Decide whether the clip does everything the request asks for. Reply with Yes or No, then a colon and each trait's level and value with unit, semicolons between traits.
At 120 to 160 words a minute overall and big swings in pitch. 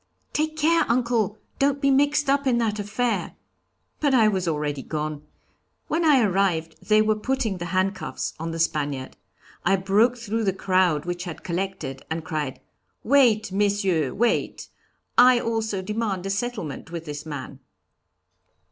Yes: average, 150 wpm; wide, 6.4 semitones